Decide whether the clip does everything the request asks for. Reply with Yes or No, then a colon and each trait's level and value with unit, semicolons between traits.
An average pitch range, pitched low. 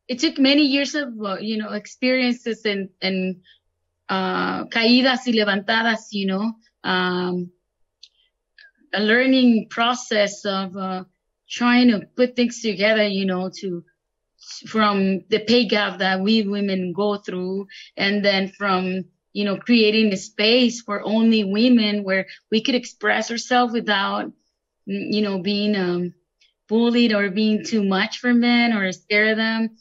No: average, 3.5 semitones; high, 210 Hz